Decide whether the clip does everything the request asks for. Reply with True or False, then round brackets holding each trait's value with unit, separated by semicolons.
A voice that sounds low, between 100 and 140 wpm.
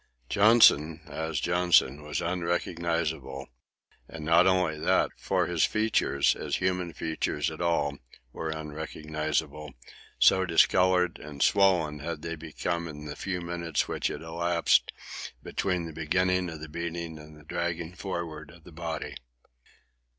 True (85 Hz; 135 wpm)